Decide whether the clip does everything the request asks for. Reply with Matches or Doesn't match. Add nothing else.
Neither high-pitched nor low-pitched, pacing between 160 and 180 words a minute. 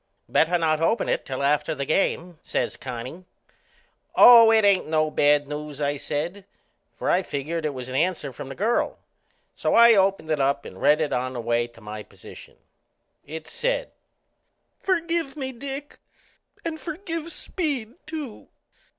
Matches